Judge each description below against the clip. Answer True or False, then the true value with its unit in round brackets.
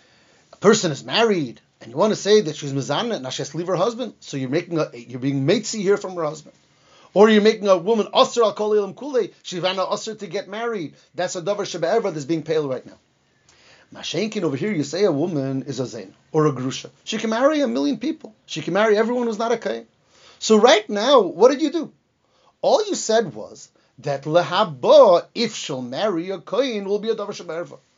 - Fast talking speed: True (220 wpm)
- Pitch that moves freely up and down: True (6.3 semitones)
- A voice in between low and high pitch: False (195 Hz)